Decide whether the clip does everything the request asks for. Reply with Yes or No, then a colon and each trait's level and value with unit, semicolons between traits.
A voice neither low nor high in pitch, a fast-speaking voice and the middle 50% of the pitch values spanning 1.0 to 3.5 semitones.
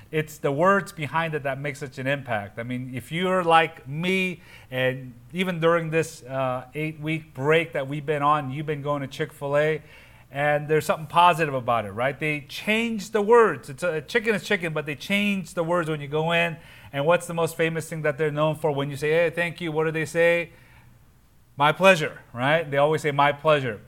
Yes: medium, 155 Hz; fast, 215 wpm; average, 3.0 semitones